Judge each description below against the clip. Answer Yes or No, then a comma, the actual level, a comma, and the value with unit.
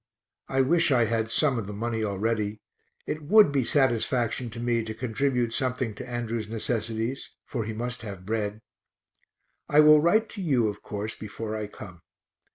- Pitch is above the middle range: No, low, 115 Hz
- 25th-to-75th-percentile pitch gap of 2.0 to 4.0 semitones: Yes, average, 3.3 semitones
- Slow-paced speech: No, average, 170 wpm